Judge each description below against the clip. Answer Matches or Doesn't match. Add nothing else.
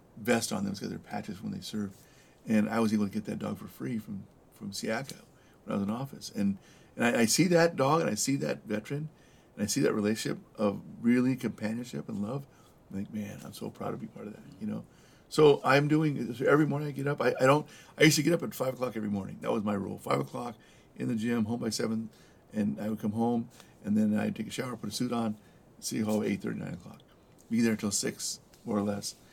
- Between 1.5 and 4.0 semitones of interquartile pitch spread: Doesn't match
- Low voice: Matches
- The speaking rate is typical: Doesn't match